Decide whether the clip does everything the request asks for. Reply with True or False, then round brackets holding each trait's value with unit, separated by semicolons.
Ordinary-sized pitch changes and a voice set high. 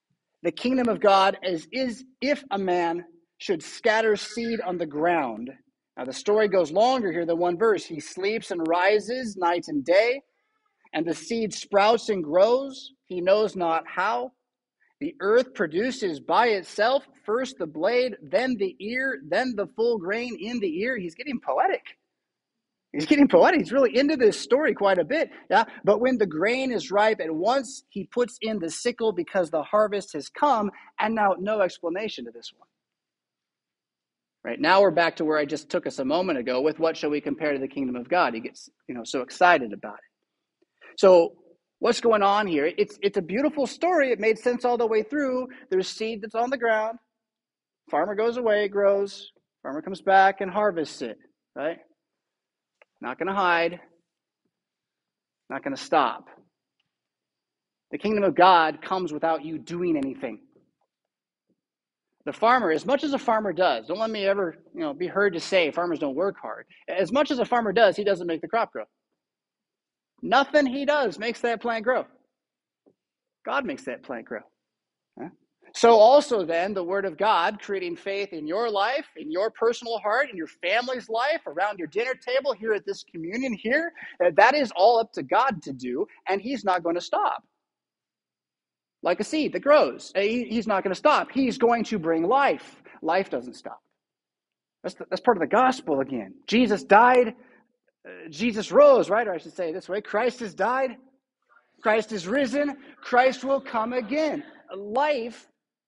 False (5.8 semitones; 220 Hz)